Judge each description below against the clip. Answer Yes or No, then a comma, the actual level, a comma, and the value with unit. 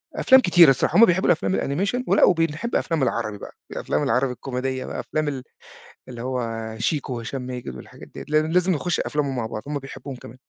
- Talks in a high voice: No, low, 135 Hz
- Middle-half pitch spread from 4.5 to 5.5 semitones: Yes, average, 5.2 semitones